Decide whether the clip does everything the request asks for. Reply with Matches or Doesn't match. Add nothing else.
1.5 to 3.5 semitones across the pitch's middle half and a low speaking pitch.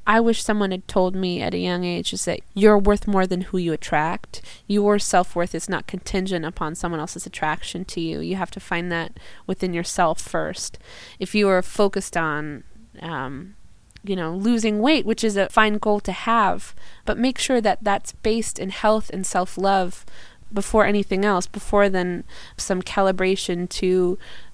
Doesn't match